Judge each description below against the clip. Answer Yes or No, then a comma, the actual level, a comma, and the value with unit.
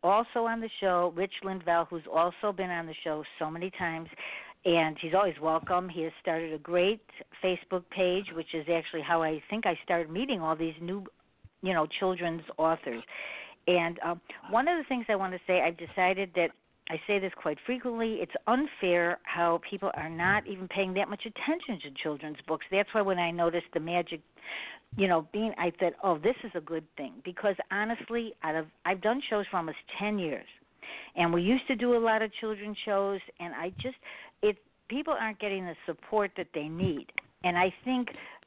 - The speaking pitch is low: No, medium, 185 Hz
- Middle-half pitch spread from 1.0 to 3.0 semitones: No, average, 3.8 semitones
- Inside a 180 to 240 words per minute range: Yes, average, 200 wpm